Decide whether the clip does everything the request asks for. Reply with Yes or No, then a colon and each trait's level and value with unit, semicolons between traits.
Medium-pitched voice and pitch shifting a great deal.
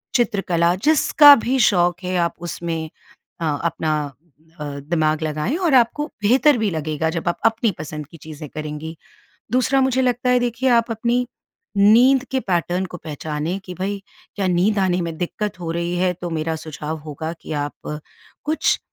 Yes: medium, 175 Hz; wide, 6.7 semitones